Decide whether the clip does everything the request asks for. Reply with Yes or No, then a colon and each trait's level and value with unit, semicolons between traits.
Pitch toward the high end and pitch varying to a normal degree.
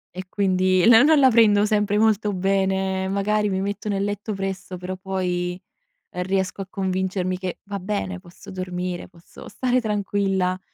No: high, 195 Hz; narrow, 1.8 semitones